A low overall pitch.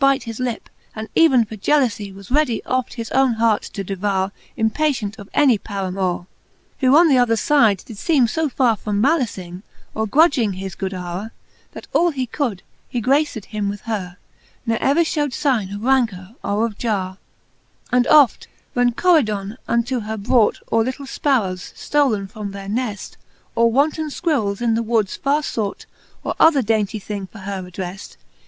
No: high, 225 Hz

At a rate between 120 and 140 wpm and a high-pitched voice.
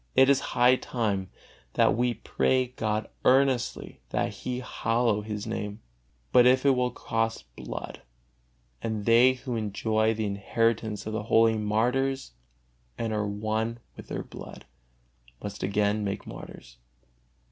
No: slow, 135 wpm; low, 115 Hz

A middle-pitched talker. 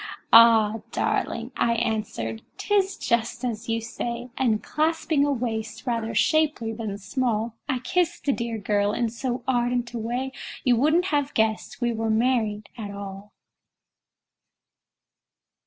No: high, 235 Hz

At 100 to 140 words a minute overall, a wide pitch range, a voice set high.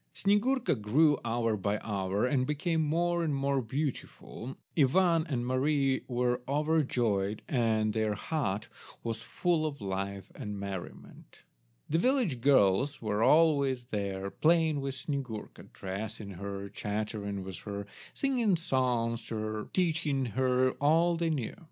No: slow, 135 wpm; wide, 6.4 semitones; low, 130 Hz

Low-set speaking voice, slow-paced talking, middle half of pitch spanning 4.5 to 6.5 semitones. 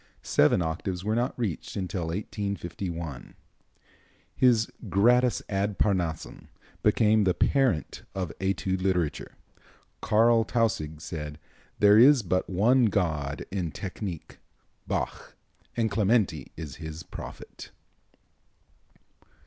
Yes: very low, 95 Hz; slow, 100 wpm; average, 4.8 semitones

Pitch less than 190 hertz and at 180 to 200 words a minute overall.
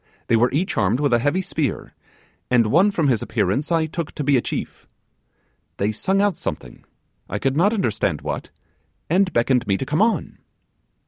Yes: medium, 140 Hz; average, 185 wpm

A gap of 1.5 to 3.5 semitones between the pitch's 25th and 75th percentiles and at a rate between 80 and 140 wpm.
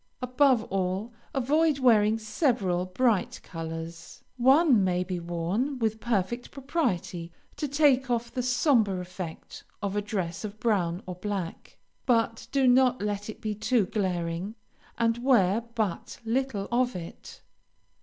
No: wide, 5.4 semitones; slow, 135 wpm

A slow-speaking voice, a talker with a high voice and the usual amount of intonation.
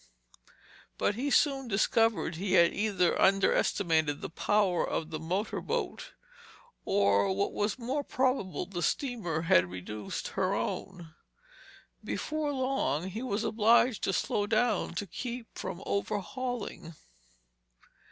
No: slow, 125 wpm; high, 200 Hz; wide, 5.7 semitones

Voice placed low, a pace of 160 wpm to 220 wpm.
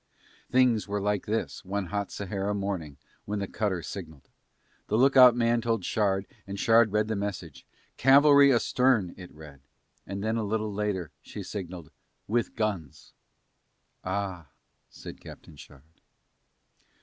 No: low, 100 Hz; slow, 135 wpm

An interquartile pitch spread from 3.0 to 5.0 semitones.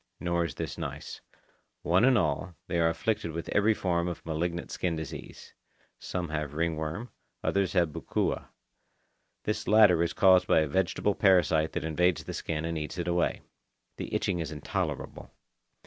No: narrow, 2.6 semitones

